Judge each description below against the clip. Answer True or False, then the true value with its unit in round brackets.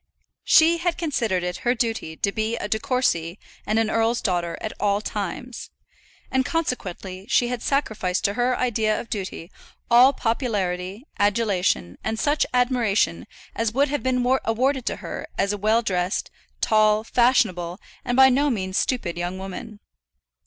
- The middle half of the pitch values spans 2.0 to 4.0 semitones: False (4.7 semitones)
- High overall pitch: True (220 Hz)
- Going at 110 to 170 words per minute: True (160 wpm)